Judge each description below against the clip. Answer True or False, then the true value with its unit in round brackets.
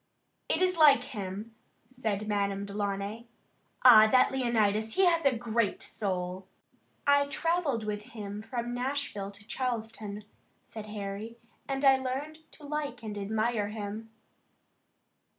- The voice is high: True (225 Hz)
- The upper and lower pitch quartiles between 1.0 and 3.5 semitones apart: False (4.3 semitones)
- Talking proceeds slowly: True (130 wpm)